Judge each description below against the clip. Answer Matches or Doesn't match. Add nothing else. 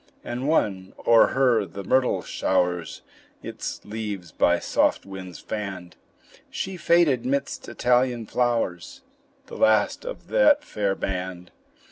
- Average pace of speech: Doesn't match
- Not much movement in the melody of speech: Doesn't match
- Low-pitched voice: Matches